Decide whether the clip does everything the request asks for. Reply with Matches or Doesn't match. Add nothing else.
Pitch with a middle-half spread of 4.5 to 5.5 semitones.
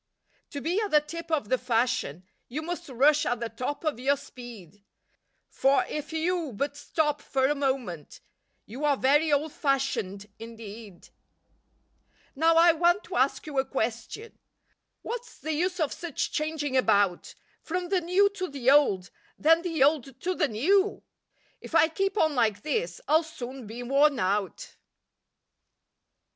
Matches